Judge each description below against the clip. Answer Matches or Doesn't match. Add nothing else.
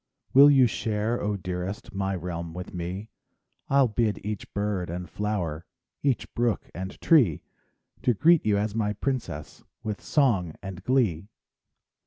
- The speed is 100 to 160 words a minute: Matches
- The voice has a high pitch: Doesn't match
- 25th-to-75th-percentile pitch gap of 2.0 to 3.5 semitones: Doesn't match